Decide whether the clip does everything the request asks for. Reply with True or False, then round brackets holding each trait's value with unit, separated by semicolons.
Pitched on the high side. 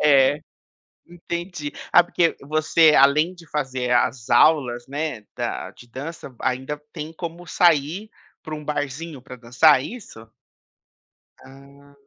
False (145 Hz)